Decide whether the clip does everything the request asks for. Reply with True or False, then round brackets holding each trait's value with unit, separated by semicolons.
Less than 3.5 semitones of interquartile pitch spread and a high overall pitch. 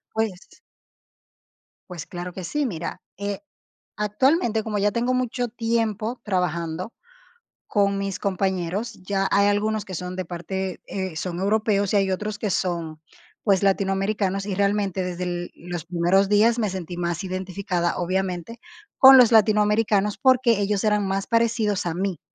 True (2.8 semitones; 195 Hz)